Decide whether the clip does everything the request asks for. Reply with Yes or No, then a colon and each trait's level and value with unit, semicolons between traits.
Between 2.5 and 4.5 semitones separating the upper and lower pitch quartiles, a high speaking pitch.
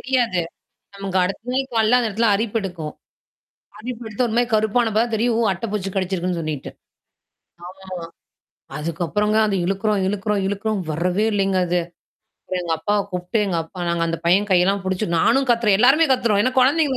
Yes: average, 4.0 semitones; high, 205 Hz